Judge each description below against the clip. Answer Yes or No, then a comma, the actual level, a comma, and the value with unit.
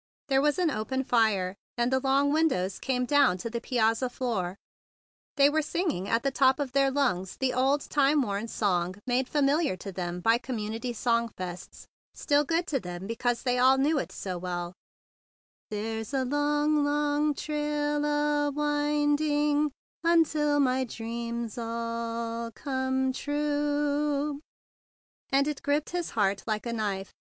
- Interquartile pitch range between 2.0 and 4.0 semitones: No, average, 4.4 semitones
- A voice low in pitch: No, very high, 265 Hz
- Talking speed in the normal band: Yes, average, 155 wpm